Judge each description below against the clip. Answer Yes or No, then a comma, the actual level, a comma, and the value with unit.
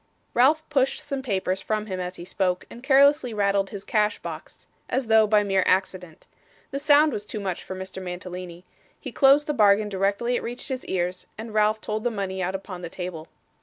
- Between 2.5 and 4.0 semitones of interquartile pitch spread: No, average, 4.6 semitones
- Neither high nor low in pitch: No, high, 205 Hz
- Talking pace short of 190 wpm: No, fast, 205 wpm